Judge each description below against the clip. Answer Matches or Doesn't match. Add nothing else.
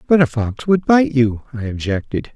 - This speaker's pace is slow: Doesn't match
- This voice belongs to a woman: Doesn't match